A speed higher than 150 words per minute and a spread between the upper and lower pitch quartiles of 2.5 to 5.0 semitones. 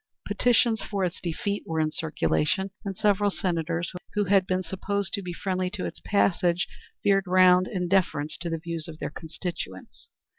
Yes: average, 175 wpm; average, 2.8 semitones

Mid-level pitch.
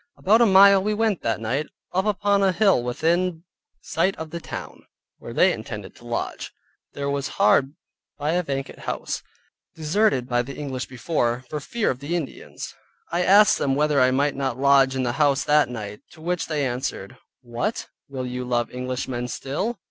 Yes: medium, 145 Hz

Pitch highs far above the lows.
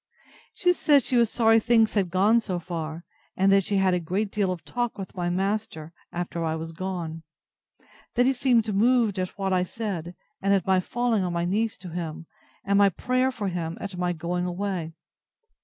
No: average, 4.0 semitones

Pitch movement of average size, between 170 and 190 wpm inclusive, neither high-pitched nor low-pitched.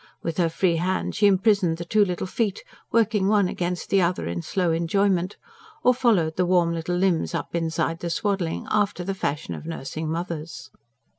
Yes: average, 3.0 semitones; average, 180 wpm; medium, 180 Hz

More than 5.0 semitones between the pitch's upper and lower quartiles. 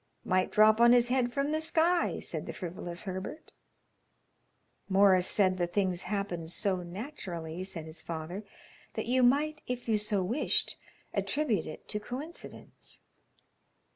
Yes: wide, 5.6 semitones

